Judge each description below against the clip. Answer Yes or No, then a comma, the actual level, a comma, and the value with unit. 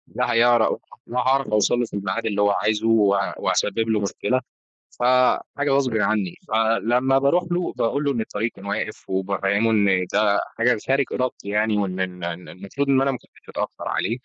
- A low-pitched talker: Yes, low, 110 Hz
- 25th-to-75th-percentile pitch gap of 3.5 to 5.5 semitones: Yes, average, 3.9 semitones